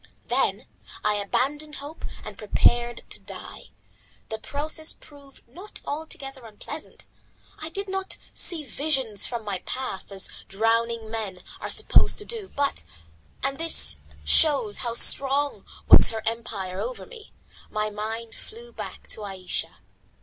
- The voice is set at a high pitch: Yes, high, 240 Hz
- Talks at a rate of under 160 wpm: Yes, average, 140 wpm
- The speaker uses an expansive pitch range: Yes, wide, 5.8 semitones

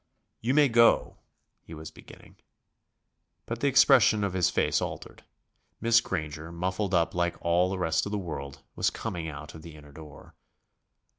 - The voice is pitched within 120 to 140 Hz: No, very low, 85 Hz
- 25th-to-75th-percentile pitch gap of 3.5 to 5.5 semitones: Yes, average, 4.9 semitones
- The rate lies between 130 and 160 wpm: No, average, 170 wpm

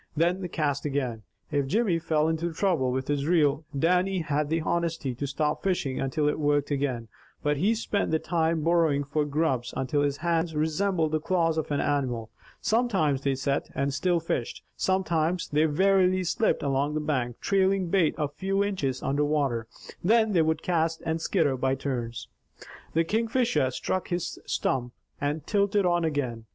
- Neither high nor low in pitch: Yes, medium, 155 Hz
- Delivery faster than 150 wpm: Yes, average, 175 wpm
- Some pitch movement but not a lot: Yes, average, 3.9 semitones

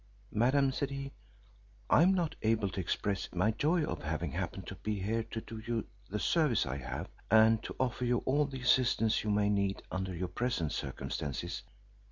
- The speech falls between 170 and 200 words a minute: Yes, average, 190 wpm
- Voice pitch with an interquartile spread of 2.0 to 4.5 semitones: No, average, 5.0 semitones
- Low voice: Yes, low, 110 Hz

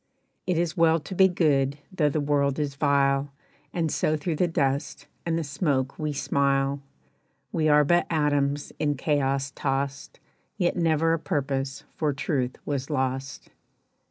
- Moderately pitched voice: Yes, medium, 145 Hz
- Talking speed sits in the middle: Yes, average, 155 wpm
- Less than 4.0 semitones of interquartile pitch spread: Yes, narrow, 2.6 semitones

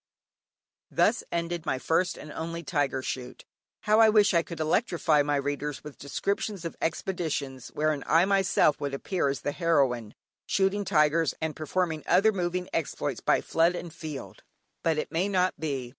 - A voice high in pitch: No, medium, 165 Hz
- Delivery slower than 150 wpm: No, average, 165 wpm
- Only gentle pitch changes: No, average, 3.8 semitones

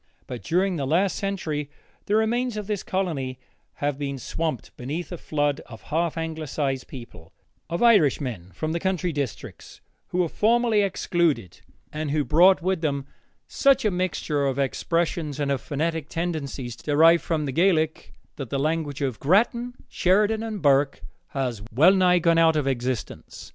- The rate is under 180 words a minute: Yes, average, 160 wpm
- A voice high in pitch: No, medium, 160 Hz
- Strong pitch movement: No, average, 4.8 semitones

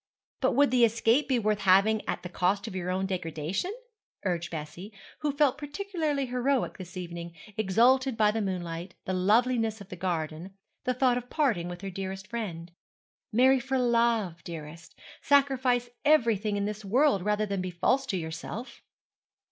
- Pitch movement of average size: No, wide, 5.7 semitones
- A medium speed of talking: Yes, average, 165 wpm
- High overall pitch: Yes, high, 210 Hz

